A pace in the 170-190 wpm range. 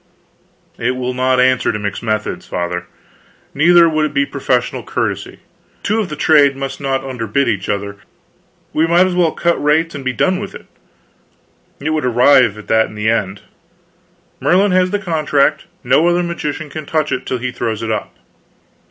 Yes: average, 180 wpm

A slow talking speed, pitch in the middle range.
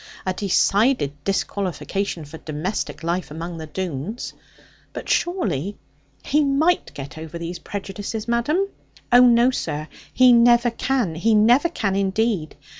No: slow, 130 wpm; high, 200 Hz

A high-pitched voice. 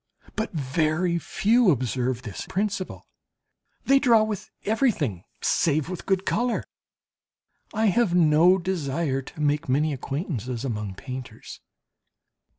No: medium, 155 Hz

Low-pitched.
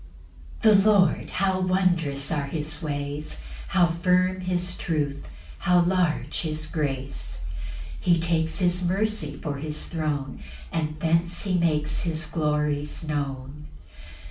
No: medium, 160 Hz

